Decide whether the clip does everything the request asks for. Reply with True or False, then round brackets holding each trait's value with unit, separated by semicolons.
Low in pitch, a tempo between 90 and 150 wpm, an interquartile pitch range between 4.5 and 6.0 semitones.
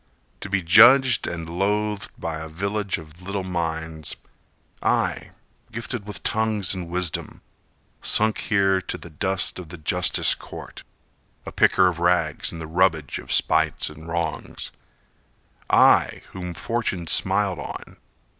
False (90 Hz; 135 wpm; 3.3 semitones)